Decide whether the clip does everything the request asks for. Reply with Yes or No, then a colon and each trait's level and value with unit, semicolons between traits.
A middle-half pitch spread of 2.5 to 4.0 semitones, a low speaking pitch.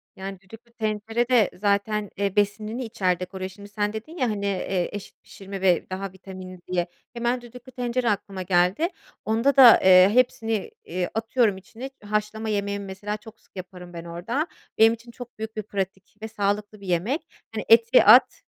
No: average, 3.1 semitones; high, 205 Hz